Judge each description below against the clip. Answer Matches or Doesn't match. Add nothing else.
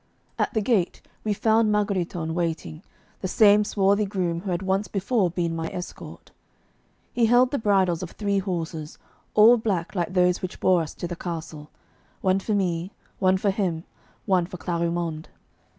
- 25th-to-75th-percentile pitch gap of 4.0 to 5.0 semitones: Doesn't match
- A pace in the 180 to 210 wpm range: Doesn't match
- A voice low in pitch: Doesn't match